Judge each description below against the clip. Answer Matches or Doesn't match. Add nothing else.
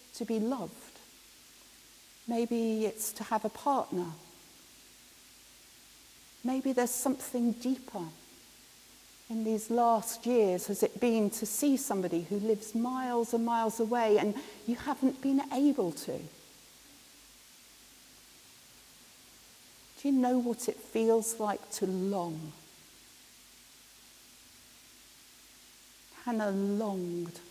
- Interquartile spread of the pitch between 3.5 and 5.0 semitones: Doesn't match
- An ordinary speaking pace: Doesn't match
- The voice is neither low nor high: Doesn't match